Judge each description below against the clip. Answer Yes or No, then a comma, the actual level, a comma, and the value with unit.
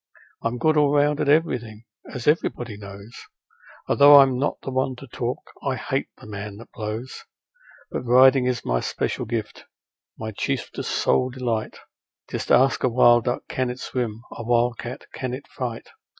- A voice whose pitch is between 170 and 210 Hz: No, low, 125 Hz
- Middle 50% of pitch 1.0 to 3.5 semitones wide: Yes, narrow, 2.6 semitones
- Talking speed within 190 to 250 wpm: No, average, 170 wpm